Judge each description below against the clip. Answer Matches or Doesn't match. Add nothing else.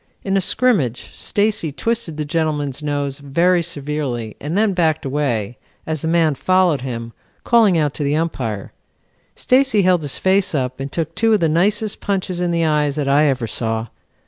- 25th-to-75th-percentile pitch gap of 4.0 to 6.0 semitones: Matches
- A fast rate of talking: Doesn't match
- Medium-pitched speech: Matches